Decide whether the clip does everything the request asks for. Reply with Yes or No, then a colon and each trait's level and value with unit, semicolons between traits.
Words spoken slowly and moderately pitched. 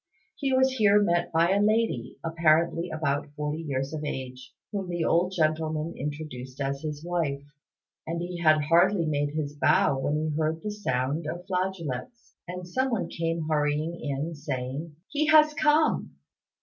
No: average, 160 wpm; medium, 160 Hz